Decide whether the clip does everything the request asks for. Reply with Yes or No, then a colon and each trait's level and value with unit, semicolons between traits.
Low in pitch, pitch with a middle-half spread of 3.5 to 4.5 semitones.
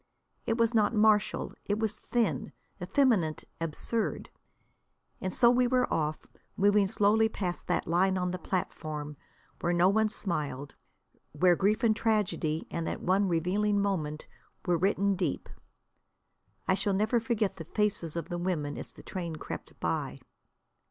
No: high, 195 Hz; average, 4.1 semitones